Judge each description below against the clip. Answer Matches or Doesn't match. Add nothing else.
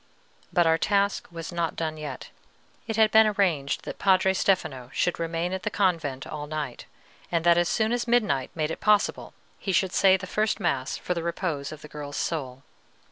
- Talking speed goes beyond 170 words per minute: Matches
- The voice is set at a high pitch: Doesn't match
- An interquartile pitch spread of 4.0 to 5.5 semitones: Matches